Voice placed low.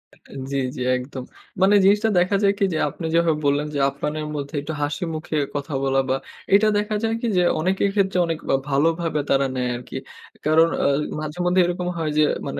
No: medium, 160 Hz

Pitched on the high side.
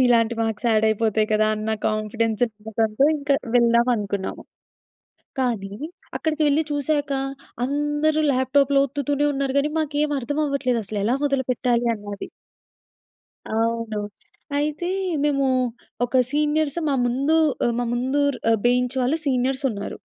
Yes: very high, 255 Hz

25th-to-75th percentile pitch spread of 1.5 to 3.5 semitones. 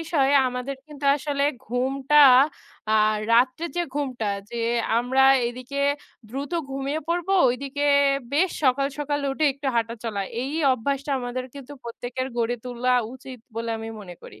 Yes: narrow, 2.6 semitones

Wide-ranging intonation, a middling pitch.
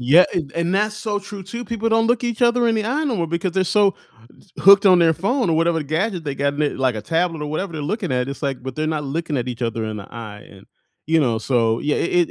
Yes: wide, 6.8 semitones; medium, 165 Hz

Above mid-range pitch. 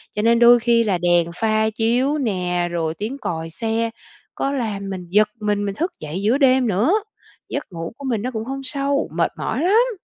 Yes: high, 220 Hz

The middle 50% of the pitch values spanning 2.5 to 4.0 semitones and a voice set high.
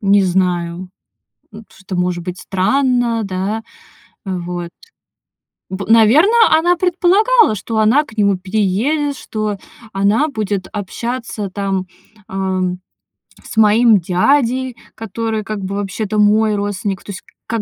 Yes: average, 3.4 semitones; high, 210 Hz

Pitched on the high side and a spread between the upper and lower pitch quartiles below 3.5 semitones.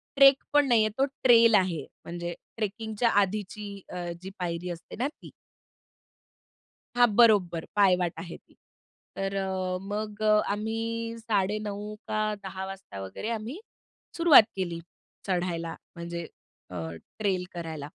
No: high, 200 Hz; average, 3.8 semitones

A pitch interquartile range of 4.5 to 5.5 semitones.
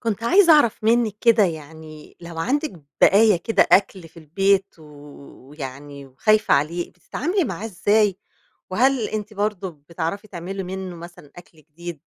Yes: average, 5.1 semitones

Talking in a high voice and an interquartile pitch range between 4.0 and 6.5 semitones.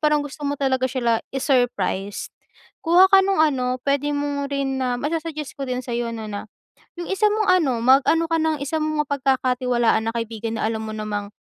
Yes: very high, 265 Hz; average, 4.3 semitones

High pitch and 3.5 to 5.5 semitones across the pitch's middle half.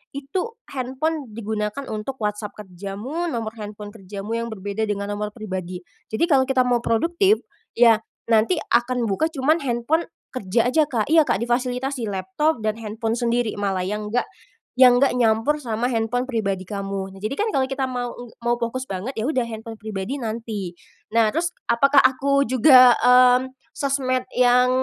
Yes: high, 235 Hz; average, 3.8 semitones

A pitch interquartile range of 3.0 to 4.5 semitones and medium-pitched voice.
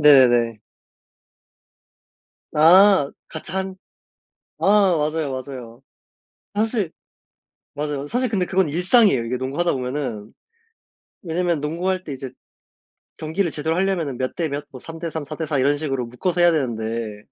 No: wide, 5.4 semitones; medium, 155 Hz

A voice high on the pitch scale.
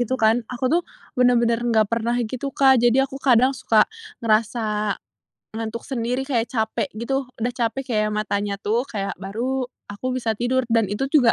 Yes: high, 235 Hz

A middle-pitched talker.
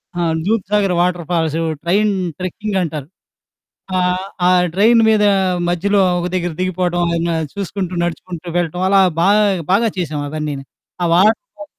Yes: medium, 180 Hz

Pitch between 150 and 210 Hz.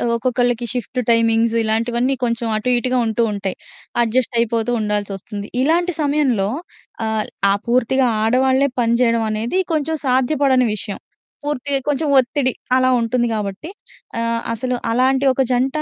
No: high, 245 Hz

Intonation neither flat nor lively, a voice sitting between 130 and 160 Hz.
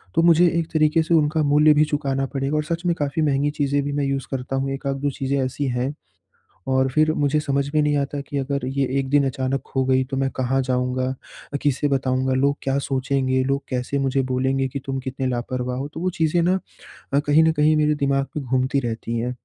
No: narrow, 2.1 semitones; medium, 140 Hz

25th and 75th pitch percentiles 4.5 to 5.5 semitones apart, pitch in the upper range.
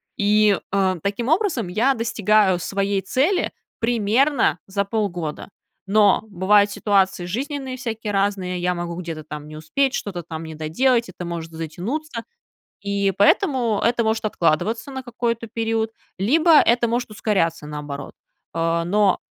Yes: average, 4.8 semitones; high, 205 Hz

